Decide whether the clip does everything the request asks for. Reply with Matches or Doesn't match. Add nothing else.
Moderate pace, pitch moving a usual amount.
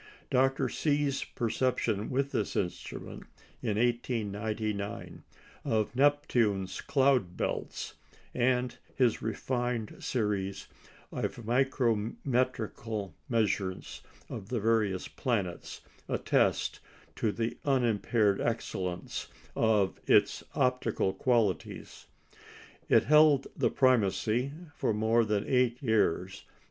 Doesn't match